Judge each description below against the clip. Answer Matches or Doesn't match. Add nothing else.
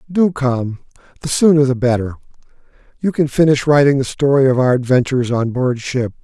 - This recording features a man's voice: Matches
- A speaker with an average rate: Matches